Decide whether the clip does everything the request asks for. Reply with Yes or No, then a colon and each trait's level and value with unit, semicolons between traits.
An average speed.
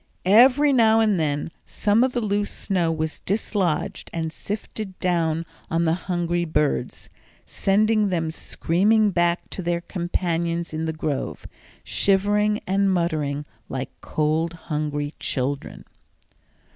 No: slow, 125 wpm